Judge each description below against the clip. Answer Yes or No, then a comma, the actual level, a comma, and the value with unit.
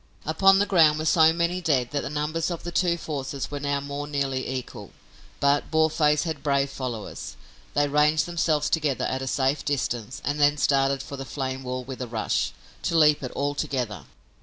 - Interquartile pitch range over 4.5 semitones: No, average, 2.8 semitones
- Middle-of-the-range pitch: Yes, medium, 145 Hz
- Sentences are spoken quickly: No, average, 195 wpm